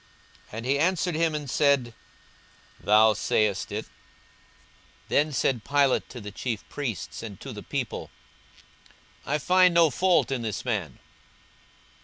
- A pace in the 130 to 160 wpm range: Yes, average, 140 wpm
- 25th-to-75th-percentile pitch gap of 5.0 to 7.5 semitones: Yes, wide, 5.6 semitones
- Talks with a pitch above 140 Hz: No, low, 135 Hz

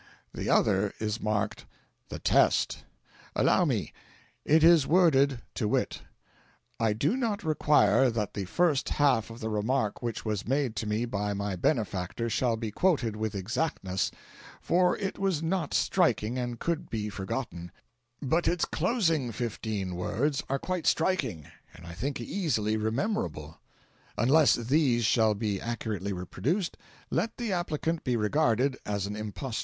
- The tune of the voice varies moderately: No, wide, 6.8 semitones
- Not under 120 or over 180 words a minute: Yes, average, 150 wpm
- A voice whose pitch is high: No, low, 120 Hz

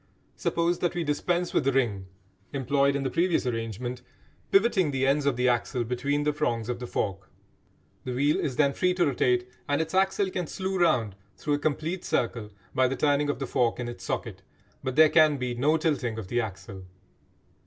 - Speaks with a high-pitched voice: No, low, 135 Hz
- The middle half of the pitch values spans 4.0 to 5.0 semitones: Yes, average, 4.4 semitones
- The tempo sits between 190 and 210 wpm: Yes, average, 200 wpm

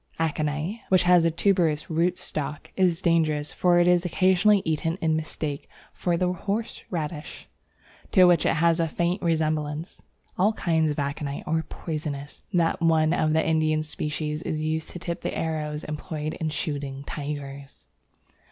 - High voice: No, medium, 160 Hz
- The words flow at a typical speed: Yes, average, 160 wpm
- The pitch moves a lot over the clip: No, narrow, 2.4 semitones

